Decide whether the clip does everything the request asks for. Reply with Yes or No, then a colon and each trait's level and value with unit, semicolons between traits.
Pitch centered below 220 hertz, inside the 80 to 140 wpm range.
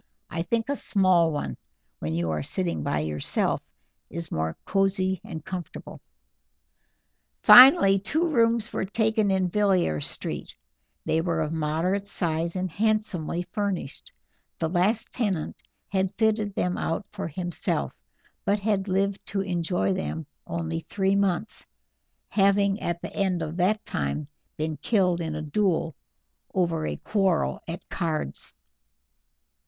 Yes: medium, 185 Hz; slow, 135 wpm